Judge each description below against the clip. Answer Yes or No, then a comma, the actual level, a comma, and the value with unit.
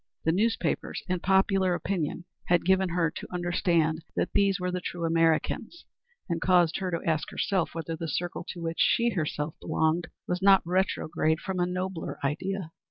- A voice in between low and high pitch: Yes, medium, 175 Hz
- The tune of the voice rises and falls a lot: No, narrow, 2.5 semitones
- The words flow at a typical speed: Yes, average, 170 wpm